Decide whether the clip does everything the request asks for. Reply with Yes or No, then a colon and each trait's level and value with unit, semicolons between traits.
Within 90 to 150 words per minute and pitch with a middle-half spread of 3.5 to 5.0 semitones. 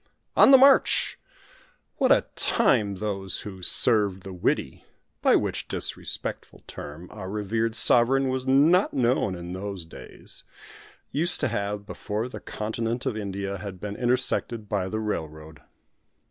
Yes: average, 140 wpm; average, 4.3 semitones